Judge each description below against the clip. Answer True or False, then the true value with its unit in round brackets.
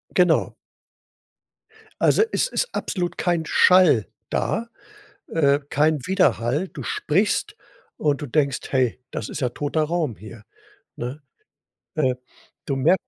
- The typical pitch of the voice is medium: True (150 Hz)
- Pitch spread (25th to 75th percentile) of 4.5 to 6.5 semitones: True (5.1 semitones)